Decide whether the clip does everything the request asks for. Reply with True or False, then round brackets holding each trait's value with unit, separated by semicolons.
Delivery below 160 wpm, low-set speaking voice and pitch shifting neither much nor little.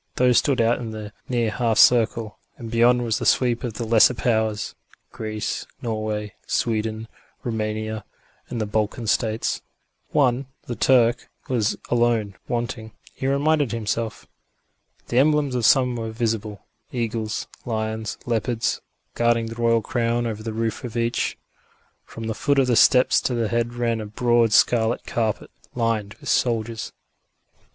False (150 wpm; 115 Hz; 1.7 semitones)